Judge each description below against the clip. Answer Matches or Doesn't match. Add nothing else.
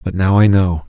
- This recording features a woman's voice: Doesn't match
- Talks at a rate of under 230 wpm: Doesn't match